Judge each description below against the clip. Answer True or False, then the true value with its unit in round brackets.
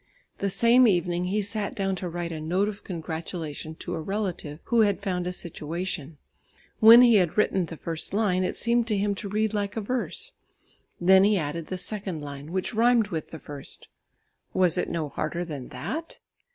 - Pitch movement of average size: True (4.2 semitones)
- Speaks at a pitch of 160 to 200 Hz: True (185 Hz)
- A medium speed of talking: True (190 wpm)